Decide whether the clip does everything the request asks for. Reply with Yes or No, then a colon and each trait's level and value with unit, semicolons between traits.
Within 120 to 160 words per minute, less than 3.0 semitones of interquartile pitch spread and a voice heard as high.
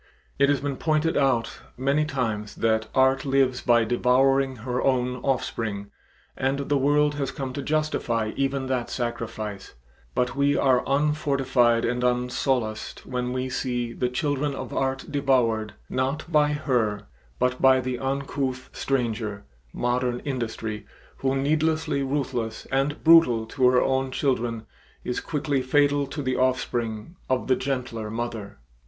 No: average, 140 wpm; narrow, 2.5 semitones; low, 130 Hz